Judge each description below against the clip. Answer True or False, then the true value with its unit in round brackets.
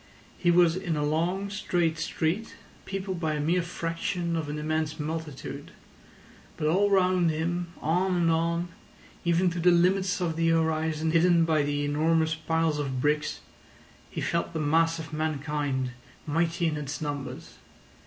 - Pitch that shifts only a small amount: True (2.1 semitones)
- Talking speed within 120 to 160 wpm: True (155 wpm)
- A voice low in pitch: False (165 Hz)